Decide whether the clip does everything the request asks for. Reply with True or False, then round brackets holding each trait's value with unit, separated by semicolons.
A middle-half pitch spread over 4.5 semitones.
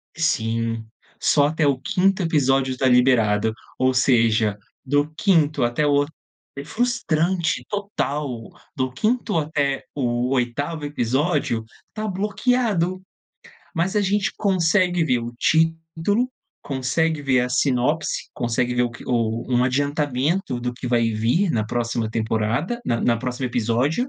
True (5.6 semitones)